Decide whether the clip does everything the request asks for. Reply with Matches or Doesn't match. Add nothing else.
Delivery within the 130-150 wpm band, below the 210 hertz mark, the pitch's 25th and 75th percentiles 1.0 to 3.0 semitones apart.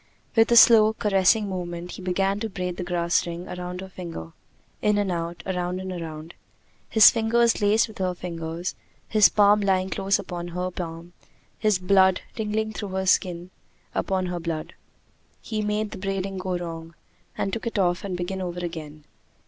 Doesn't match